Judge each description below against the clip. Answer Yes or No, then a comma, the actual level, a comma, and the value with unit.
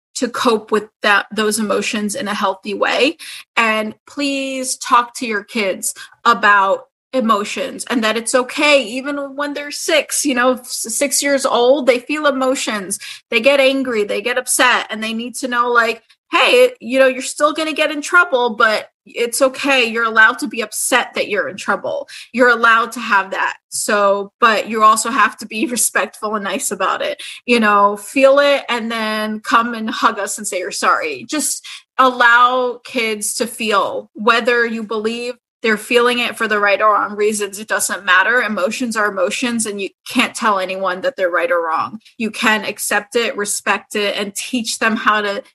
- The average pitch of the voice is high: Yes, high, 235 Hz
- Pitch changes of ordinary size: Yes, average, 3.7 semitones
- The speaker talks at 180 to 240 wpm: Yes, average, 190 wpm